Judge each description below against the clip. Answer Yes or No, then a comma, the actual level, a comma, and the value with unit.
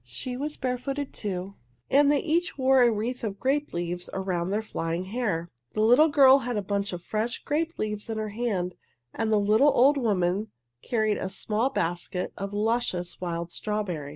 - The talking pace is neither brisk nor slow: Yes, average, 180 wpm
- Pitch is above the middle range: Yes, high, 215 Hz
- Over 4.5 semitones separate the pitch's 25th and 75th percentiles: Yes, wide, 5.5 semitones